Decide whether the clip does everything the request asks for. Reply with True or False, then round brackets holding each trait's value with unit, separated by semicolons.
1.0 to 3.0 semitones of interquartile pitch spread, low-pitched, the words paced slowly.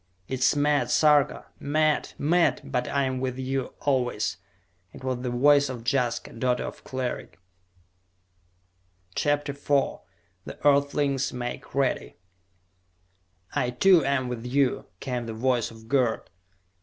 True (2.5 semitones; 130 Hz; 130 wpm)